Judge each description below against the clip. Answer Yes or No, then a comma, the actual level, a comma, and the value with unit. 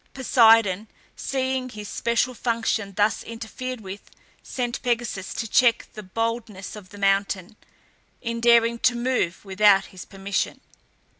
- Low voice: No, high, 225 Hz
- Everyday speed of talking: No, slow, 130 wpm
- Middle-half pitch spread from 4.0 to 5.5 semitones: No, average, 3.2 semitones